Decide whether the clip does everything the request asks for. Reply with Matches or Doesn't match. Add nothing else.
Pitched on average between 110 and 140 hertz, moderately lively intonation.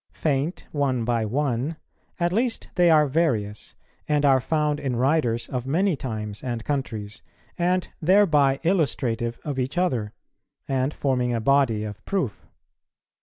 Matches